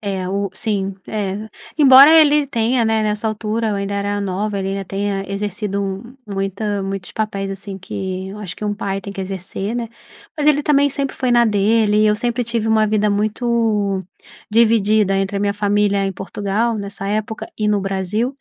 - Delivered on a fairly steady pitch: Yes, narrow, 2.1 semitones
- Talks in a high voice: Yes, high, 205 Hz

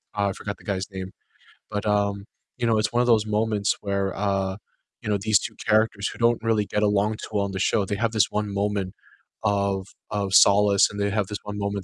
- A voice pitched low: Yes, low, 100 Hz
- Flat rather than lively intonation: Yes, narrow, 1.3 semitones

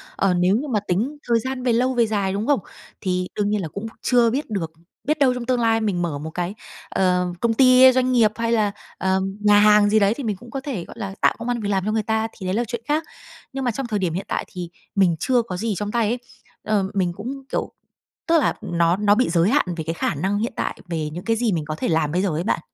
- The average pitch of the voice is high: Yes, high, 210 Hz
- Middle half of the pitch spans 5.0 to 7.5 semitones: No, average, 4.6 semitones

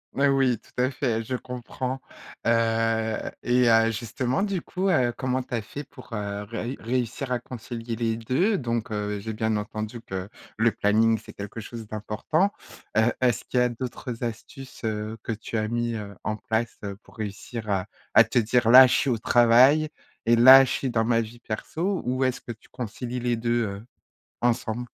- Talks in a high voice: No, low, 115 Hz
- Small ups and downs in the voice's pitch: Yes, narrow, 2.3 semitones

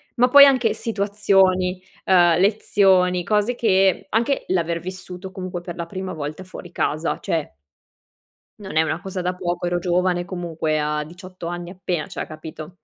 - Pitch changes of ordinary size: No, narrow, 2.0 semitones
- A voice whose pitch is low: No, medium, 180 Hz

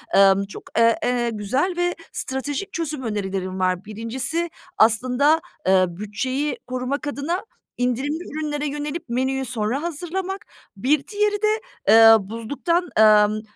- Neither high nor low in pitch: No, very high, 260 Hz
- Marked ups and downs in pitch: Yes, wide, 6.0 semitones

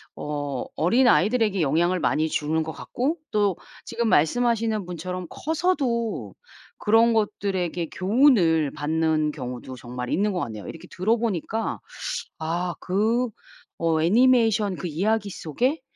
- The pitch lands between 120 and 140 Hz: No, medium, 185 Hz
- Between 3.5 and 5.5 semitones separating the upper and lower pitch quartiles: No, wide, 6.2 semitones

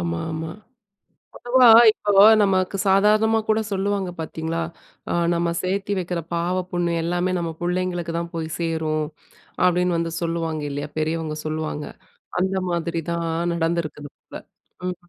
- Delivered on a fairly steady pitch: Yes, narrow, 2.3 semitones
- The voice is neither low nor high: Yes, medium, 170 Hz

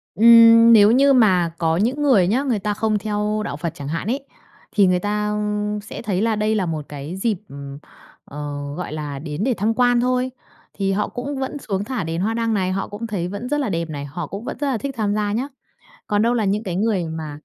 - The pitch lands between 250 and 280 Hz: No, high, 210 Hz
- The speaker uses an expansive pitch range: No, average, 4.7 semitones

